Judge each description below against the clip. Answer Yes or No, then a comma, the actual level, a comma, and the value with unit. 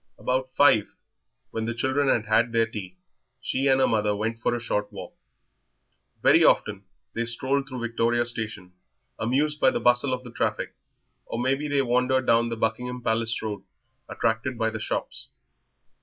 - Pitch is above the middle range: No, low, 120 Hz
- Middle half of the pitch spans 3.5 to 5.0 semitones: No, narrow, 2.6 semitones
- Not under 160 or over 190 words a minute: Yes, average, 170 wpm